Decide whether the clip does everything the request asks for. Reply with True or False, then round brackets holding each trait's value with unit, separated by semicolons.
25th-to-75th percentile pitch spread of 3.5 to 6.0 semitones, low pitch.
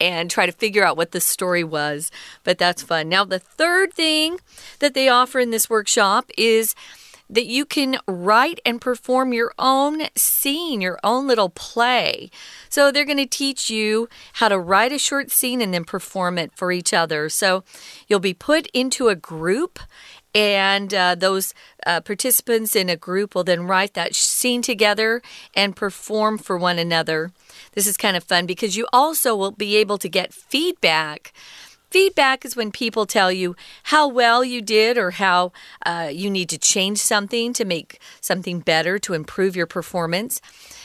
False (5.6 semitones; 210 Hz)